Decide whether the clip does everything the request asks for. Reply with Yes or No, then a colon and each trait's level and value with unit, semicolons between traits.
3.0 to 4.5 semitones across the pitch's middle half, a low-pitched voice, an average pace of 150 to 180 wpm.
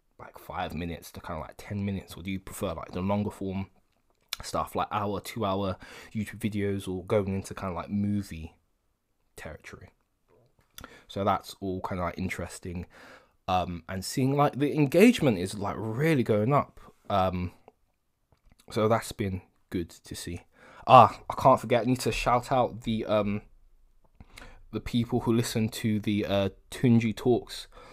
Yes: average, 3.4 semitones; low, 100 Hz; average, 165 wpm